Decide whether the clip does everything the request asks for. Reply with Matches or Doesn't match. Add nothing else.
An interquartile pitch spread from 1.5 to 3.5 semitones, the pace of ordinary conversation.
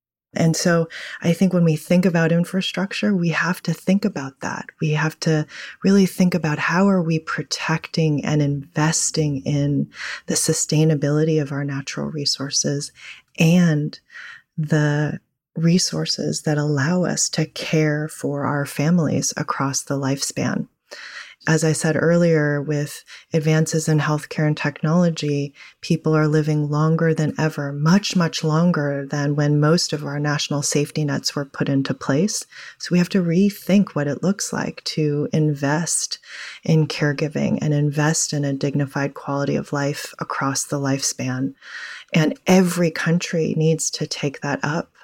Matches